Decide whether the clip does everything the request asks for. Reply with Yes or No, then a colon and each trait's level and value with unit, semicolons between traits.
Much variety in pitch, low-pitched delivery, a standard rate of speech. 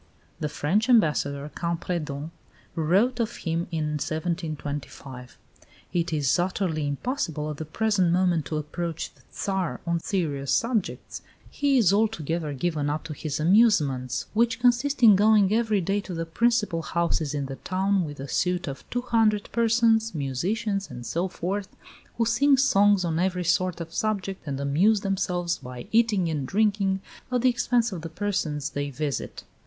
No: wide, 5.7 semitones; medium, 180 Hz; average, 160 wpm